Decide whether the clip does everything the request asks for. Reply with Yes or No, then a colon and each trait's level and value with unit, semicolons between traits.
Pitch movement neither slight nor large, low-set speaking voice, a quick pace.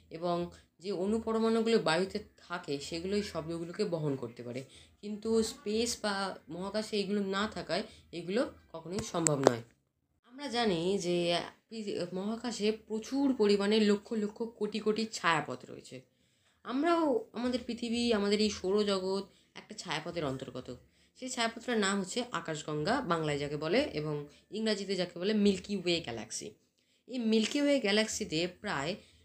No: average, 4.7 semitones; high, 205 Hz; fast, 125 wpm